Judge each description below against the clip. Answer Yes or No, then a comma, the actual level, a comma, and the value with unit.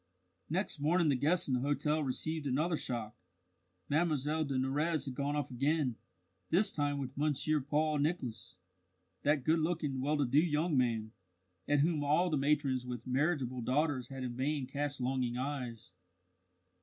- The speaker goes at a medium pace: Yes, average, 160 wpm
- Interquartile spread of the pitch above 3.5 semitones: No, average, 3.1 semitones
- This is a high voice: No, medium, 145 Hz